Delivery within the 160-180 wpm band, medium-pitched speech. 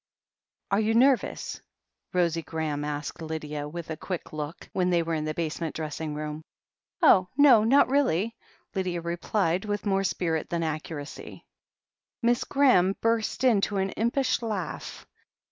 No: average, 145 wpm; medium, 175 Hz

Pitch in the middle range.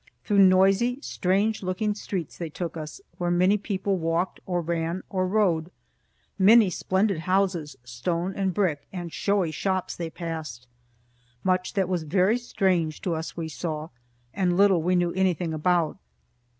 Yes: medium, 180 Hz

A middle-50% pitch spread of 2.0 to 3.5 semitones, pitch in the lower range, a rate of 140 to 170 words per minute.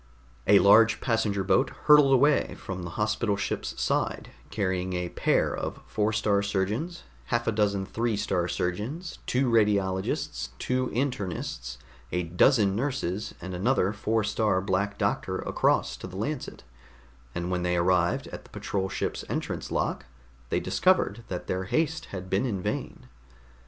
No: average, 4.0 semitones; low, 100 Hz; average, 150 wpm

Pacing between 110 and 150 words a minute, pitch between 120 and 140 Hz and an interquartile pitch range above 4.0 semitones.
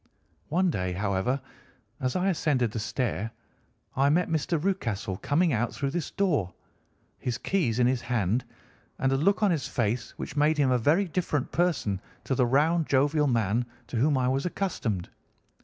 No: average, 175 wpm; low, 135 Hz; wide, 5.6 semitones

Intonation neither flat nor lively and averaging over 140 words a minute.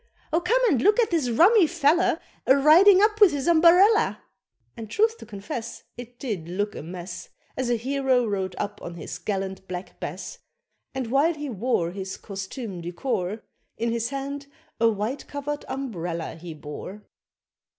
No: wide, 7.5 semitones; average, 170 wpm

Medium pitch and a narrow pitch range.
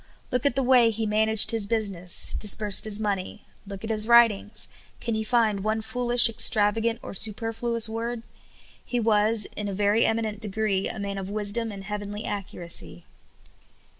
No: high, 215 Hz; narrow, 1.9 semitones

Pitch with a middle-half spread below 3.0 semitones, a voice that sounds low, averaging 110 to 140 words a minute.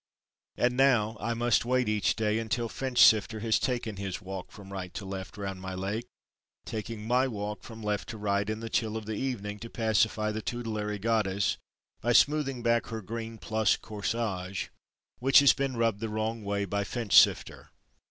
No: narrow, 2.4 semitones; low, 110 Hz; average, 180 wpm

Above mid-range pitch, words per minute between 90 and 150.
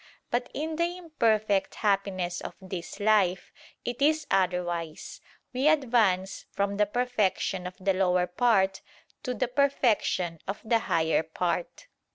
Yes: high, 200 Hz; slow, 135 wpm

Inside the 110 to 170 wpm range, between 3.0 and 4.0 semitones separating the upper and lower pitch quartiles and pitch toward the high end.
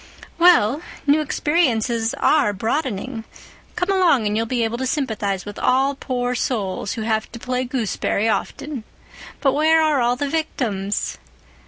No: average, 150 wpm; average, 4.7 semitones; very high, 250 Hz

